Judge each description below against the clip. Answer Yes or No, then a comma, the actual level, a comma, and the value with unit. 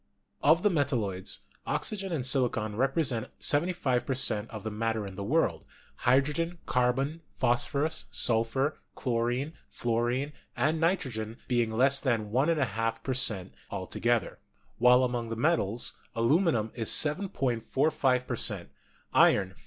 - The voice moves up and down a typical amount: Yes, average, 4.4 semitones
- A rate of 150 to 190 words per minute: No, slow, 135 wpm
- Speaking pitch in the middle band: No, low, 125 Hz